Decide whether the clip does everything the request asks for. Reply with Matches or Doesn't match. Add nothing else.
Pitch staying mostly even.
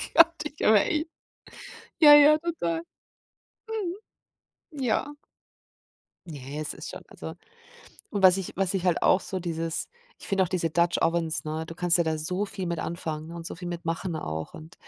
Doesn't match